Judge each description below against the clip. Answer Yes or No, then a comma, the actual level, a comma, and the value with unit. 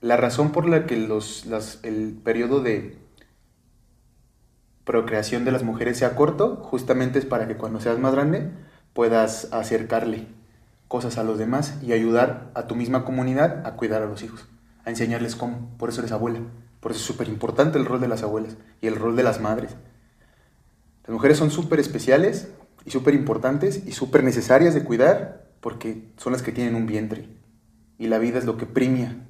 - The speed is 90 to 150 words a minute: No, average, 185 wpm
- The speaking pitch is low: Yes, low, 115 Hz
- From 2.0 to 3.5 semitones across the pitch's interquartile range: Yes, narrow, 2.5 semitones